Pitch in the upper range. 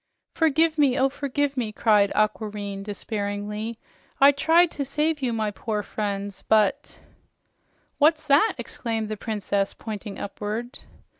Yes: high, 225 Hz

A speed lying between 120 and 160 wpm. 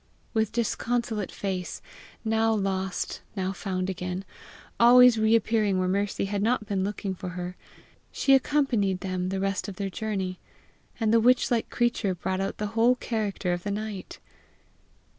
Yes: average, 155 wpm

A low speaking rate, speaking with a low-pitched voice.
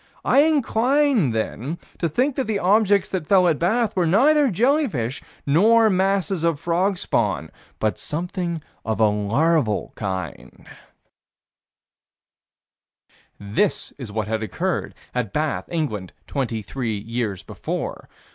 No: slow, 120 wpm; medium, 165 Hz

